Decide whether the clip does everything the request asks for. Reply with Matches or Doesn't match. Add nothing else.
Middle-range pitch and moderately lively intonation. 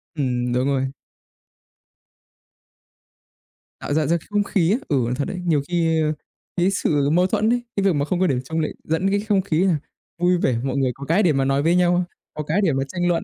Matches